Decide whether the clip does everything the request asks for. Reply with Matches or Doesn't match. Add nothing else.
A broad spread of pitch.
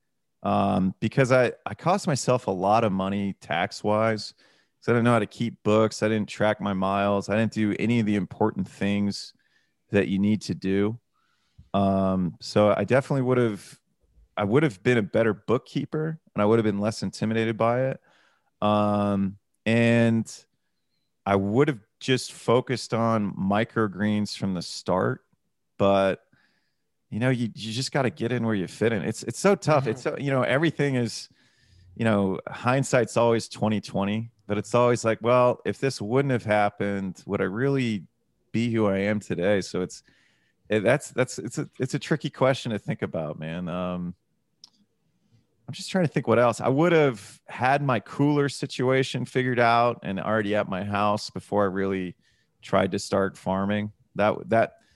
Doesn't match